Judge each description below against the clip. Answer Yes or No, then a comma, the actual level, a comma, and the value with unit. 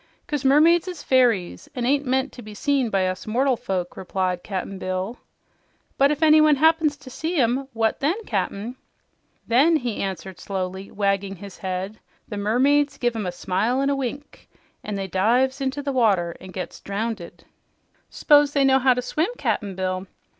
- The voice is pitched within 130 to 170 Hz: No, high, 235 Hz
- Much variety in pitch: Yes, wide, 6.3 semitones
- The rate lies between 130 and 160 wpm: No, average, 175 wpm